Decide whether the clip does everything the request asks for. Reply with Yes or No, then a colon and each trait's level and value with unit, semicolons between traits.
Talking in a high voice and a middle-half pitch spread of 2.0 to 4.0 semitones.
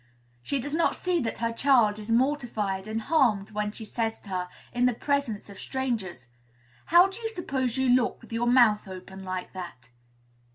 No: high, 230 Hz; average, 4.5 semitones